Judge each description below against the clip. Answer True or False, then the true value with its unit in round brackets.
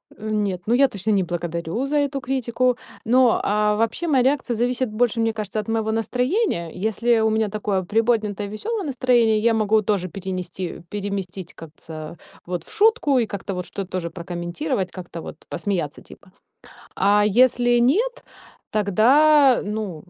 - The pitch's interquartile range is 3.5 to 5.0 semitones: True (4.6 semitones)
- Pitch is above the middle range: True (215 Hz)